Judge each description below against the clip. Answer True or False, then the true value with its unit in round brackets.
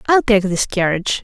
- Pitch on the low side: False (205 Hz)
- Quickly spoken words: False (195 wpm)